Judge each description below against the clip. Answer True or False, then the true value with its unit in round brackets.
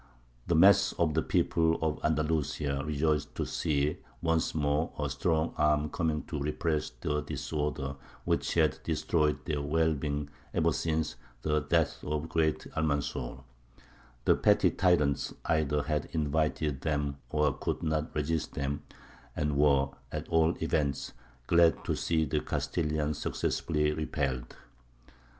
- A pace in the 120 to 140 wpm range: True (135 wpm)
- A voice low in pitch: True (75 Hz)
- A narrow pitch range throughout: True (1.7 semitones)